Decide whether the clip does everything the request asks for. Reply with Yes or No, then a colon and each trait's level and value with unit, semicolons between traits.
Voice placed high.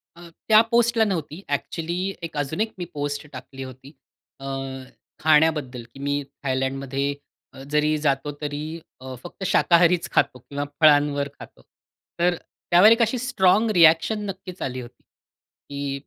No: medium, 150 Hz